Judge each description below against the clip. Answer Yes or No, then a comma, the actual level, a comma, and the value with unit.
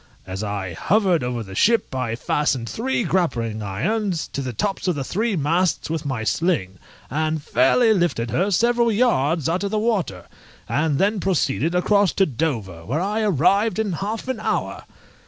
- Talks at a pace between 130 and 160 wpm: No, average, 175 wpm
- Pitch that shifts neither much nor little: No, wide, 8.3 semitones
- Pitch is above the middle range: No, medium, 165 Hz